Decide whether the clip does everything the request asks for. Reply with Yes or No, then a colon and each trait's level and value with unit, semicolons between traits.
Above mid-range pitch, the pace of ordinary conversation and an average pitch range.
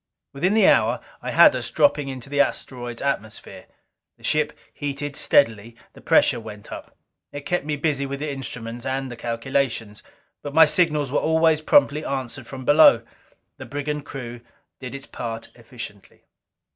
No: medium, 140 Hz; average, 160 wpm; average, 3.7 semitones